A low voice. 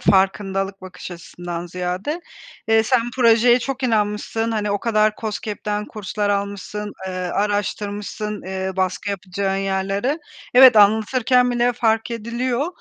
No: high, 210 Hz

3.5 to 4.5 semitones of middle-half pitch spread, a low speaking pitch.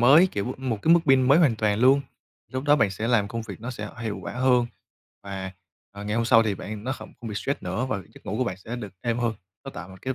Yes: average, 3.8 semitones; low, 115 Hz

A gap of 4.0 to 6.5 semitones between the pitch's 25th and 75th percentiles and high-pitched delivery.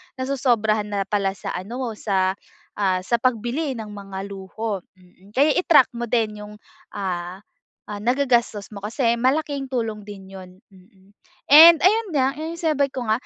Yes: average, 5.0 semitones; high, 220 Hz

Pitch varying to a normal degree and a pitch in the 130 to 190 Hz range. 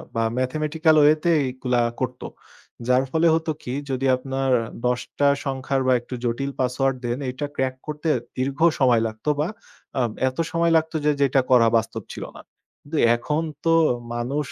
Yes: average, 3.1 semitones; low, 135 Hz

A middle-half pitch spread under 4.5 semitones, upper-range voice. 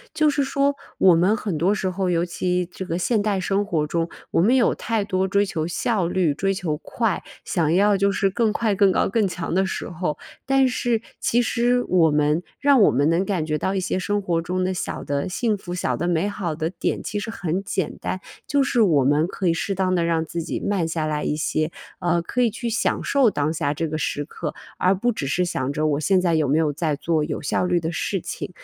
No: average, 4.1 semitones; medium, 180 Hz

